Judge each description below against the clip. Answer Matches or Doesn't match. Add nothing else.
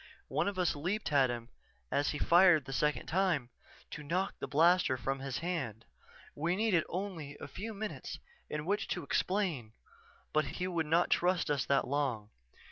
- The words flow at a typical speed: Matches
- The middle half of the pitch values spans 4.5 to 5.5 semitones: Matches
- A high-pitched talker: Doesn't match